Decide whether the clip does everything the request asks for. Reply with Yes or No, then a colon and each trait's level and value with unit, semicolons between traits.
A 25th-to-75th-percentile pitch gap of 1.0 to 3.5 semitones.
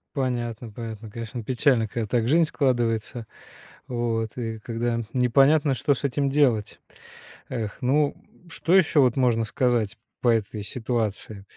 Yes: average, 2.9 semitones